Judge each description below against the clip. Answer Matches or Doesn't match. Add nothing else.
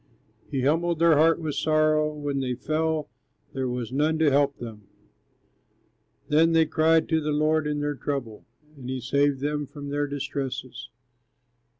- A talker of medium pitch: Matches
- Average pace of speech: Matches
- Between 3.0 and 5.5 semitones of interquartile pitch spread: Doesn't match